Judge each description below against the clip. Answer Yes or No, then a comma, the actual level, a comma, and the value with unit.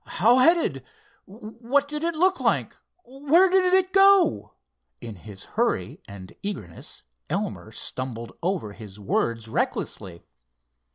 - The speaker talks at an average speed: No, slow, 120 wpm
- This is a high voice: Yes, high, 215 Hz